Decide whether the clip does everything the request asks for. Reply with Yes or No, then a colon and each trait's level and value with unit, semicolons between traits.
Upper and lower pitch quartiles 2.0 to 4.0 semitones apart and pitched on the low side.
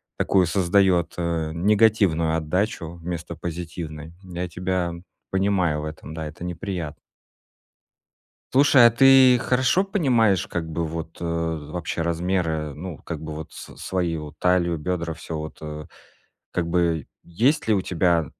Yes: average, 2.9 semitones; very low, 85 Hz